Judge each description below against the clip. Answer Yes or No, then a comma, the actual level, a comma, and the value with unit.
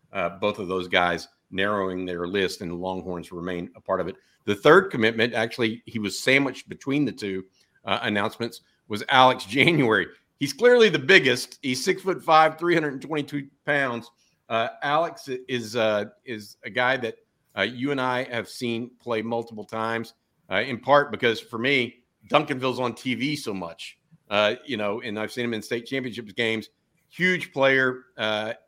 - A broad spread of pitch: No, average, 4.5 semitones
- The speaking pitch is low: Yes, low, 120 Hz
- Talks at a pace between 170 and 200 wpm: Yes, average, 180 wpm